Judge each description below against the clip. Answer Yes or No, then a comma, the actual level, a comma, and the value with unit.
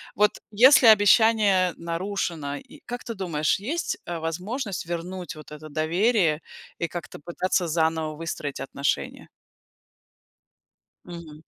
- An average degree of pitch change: Yes, average, 4.4 semitones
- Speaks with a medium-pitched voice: Yes, medium, 175 Hz